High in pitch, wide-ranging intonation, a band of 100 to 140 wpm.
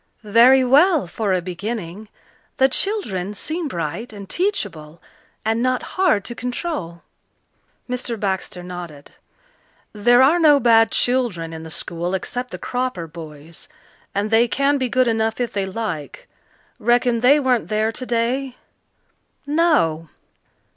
Yes: high, 225 Hz; wide, 6.0 semitones; slow, 135 wpm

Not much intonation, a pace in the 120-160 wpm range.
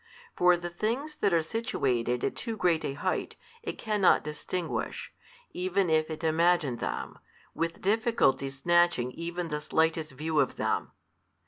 No: average, 3.4 semitones; average, 145 wpm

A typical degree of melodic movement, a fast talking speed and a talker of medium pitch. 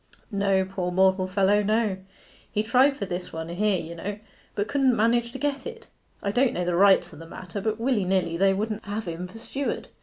No: average, 3.6 semitones; fast, 215 wpm; high, 200 Hz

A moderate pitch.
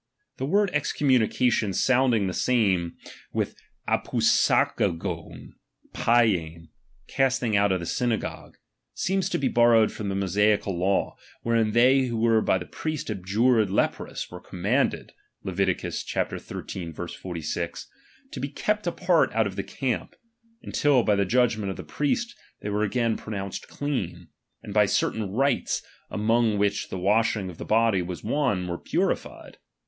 No: low, 110 Hz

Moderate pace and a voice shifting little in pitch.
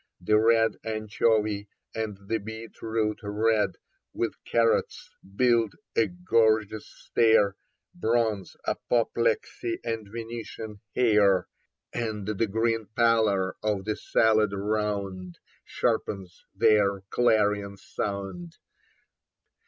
No: slow, 100 wpm; narrow, 2.0 semitones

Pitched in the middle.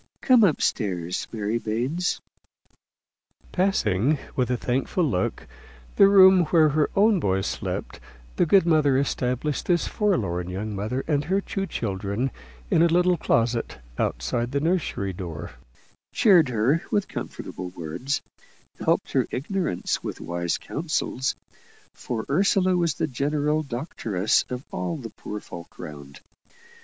No: low, 130 Hz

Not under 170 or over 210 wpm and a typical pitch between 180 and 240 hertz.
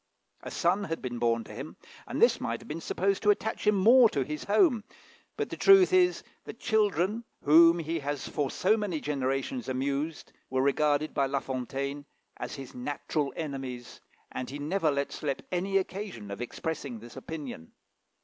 No: average, 175 wpm; medium, 150 Hz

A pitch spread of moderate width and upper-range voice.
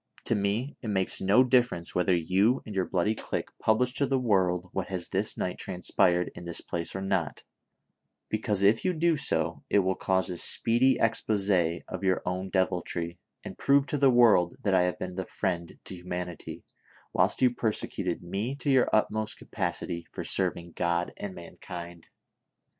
No: average, 4.1 semitones; very low, 95 Hz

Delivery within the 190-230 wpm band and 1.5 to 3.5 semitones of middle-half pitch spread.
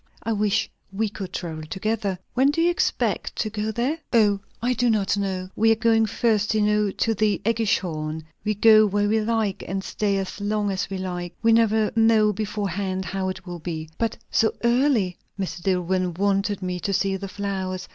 Yes: average, 200 wpm; average, 2.8 semitones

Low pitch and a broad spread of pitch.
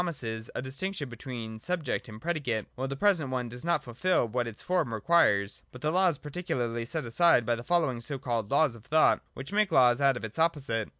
Yes: low, 130 Hz; wide, 5.8 semitones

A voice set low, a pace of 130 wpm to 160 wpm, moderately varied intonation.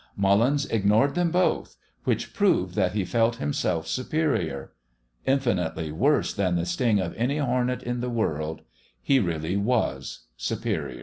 No: low, 110 Hz; average, 140 wpm; wide, 6.5 semitones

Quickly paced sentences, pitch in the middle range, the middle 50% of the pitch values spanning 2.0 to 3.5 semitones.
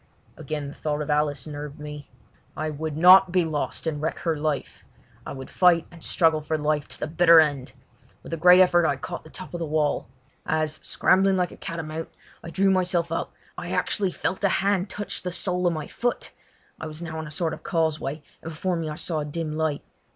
Yes: fast, 220 wpm; medium, 160 Hz; average, 2.7 semitones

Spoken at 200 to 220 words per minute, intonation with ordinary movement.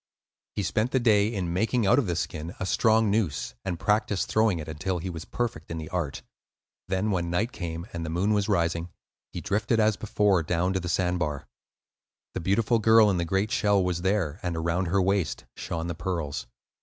Yes: fast, 205 wpm; average, 3.8 semitones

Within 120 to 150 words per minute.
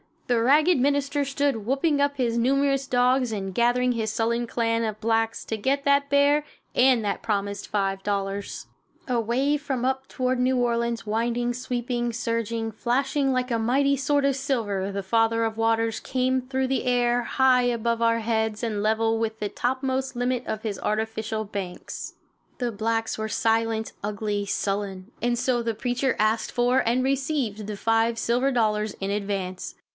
No: average, 165 wpm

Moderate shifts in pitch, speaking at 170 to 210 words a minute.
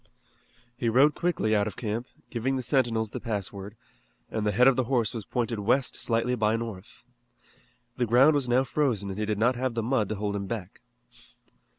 Yes: average, 3.2 semitones; fast, 205 wpm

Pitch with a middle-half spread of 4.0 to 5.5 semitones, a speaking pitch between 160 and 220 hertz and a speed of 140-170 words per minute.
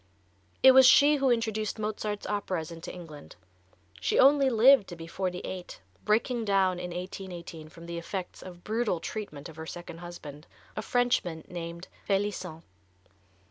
Yes: average, 4.4 semitones; medium, 185 Hz; average, 150 wpm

